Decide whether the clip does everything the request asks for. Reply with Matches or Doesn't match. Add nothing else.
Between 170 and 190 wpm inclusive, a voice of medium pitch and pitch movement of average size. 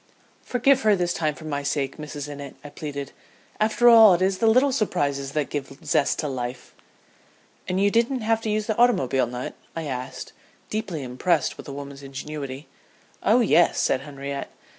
Doesn't match